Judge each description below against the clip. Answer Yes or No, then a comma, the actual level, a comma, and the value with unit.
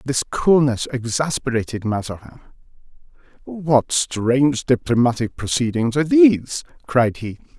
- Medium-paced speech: No, slow, 95 wpm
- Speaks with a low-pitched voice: Yes, low, 130 Hz